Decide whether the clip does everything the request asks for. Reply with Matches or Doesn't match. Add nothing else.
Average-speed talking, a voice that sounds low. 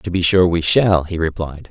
Doesn't match